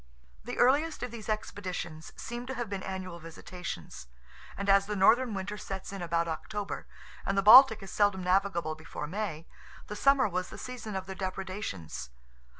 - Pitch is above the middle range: Yes, high, 195 Hz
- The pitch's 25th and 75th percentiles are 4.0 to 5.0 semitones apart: No, average, 3.1 semitones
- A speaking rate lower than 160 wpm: No, average, 170 wpm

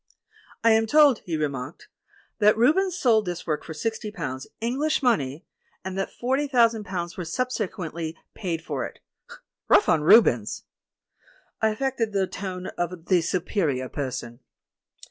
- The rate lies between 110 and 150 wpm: Yes, average, 145 wpm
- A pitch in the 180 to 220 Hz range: Yes, high, 190 Hz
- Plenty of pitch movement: Yes, wide, 6.1 semitones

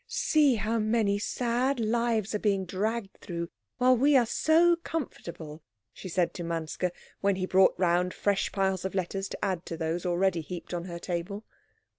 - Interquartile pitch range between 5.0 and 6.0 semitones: No, average, 4.6 semitones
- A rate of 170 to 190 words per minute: Yes, average, 175 wpm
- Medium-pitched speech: No, high, 195 Hz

